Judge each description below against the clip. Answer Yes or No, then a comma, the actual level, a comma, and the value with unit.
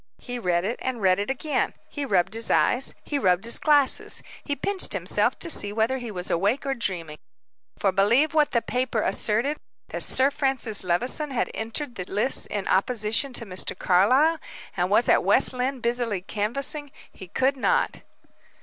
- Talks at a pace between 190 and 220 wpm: No, average, 175 wpm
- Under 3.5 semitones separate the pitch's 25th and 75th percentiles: No, average, 5.2 semitones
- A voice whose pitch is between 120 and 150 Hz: No, high, 235 Hz